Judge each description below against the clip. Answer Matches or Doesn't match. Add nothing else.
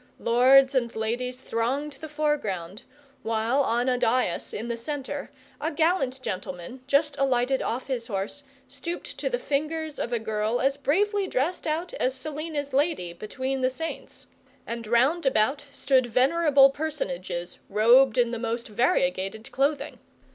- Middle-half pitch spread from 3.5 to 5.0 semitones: Matches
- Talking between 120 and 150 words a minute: Matches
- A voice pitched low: Doesn't match